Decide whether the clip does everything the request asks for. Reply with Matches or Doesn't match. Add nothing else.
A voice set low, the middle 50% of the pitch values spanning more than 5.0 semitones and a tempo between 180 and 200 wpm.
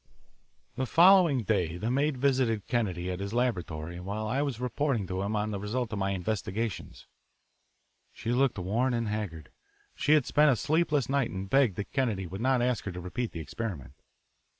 Matches